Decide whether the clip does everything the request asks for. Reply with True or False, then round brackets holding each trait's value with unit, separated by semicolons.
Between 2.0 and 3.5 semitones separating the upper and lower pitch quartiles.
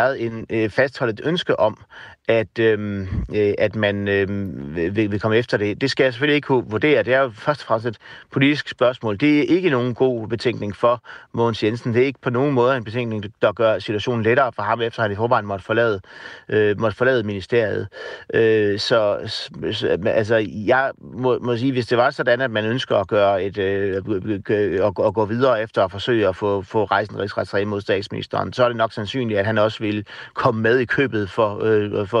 True (3.1 semitones)